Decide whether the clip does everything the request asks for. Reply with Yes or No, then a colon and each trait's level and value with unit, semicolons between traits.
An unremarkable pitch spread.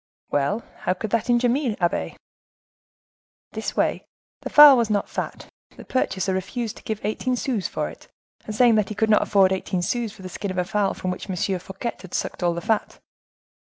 Yes: average, 3.9 semitones